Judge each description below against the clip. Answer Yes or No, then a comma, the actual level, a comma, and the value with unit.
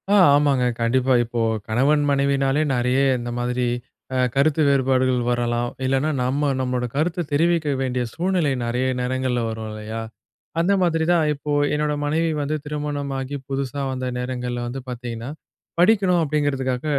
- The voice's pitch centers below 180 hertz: Yes, low, 135 Hz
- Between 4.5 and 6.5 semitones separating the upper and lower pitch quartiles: No, average, 3.1 semitones